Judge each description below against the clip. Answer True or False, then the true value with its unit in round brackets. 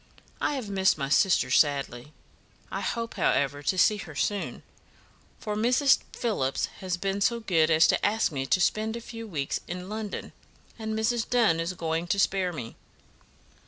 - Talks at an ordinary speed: True (170 wpm)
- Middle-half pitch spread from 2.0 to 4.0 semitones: False (5.6 semitones)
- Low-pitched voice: False (190 Hz)